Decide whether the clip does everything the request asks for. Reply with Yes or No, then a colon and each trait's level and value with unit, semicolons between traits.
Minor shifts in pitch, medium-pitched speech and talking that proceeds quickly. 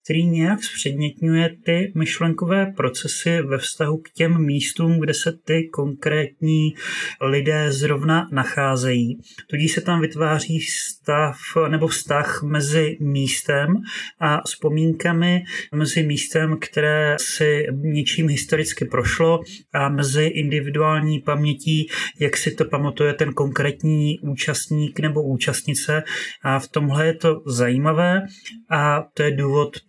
No: narrow, 1.8 semitones; medium, 155 Hz; average, 120 wpm